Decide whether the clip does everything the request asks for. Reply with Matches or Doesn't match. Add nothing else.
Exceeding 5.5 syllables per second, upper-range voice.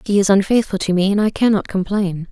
Matches